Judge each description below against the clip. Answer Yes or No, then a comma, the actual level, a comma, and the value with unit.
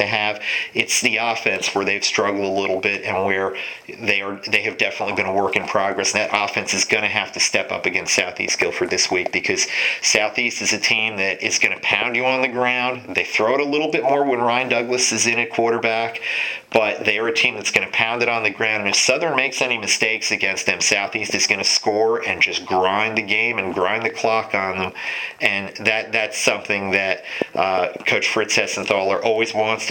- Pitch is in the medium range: No, low, 110 Hz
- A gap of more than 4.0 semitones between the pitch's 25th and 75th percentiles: No, average, 2.8 semitones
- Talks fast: Yes, fast, 225 wpm